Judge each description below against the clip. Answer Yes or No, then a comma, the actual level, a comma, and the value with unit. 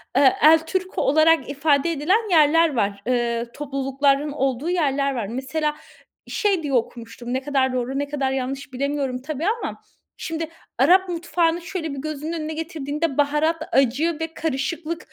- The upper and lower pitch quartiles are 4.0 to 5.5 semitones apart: No, average, 3.5 semitones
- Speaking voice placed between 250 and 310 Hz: Yes, very high, 290 Hz